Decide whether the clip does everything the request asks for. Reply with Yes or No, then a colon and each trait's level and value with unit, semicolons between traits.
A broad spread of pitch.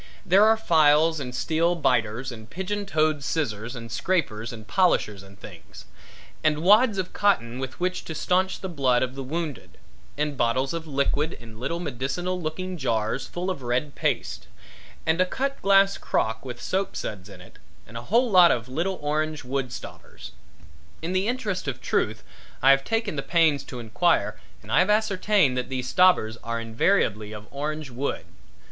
Yes: wide, 7.1 semitones